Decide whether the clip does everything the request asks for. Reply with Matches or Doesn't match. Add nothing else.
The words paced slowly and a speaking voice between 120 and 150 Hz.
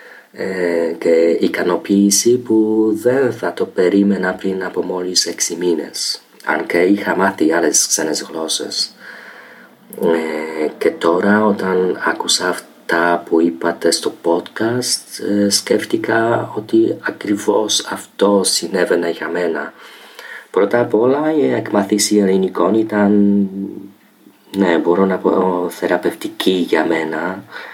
Doesn't match